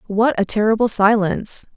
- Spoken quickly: No, slow, 135 wpm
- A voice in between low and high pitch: No, high, 215 Hz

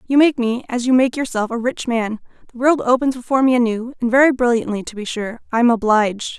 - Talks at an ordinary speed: No, fast, 225 wpm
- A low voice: No, high, 240 Hz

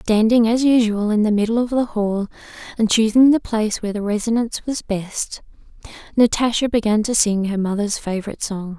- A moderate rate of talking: Yes, average, 180 wpm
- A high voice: Yes, high, 220 Hz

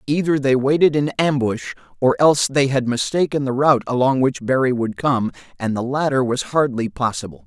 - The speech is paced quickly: No, average, 185 wpm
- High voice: No, low, 130 Hz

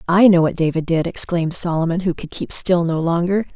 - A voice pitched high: No, medium, 170 Hz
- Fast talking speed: Yes, fast, 220 wpm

